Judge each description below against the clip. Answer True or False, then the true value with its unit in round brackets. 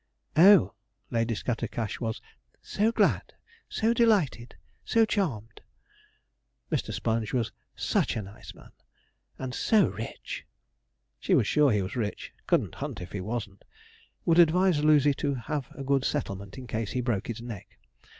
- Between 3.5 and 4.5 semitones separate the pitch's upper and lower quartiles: False (5.6 semitones)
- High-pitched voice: False (120 Hz)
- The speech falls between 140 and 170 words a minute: True (150 wpm)